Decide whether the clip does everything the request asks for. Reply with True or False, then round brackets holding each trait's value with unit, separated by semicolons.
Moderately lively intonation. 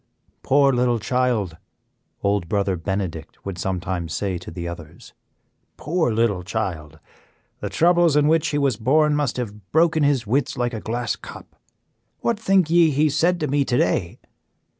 False (7.6 semitones)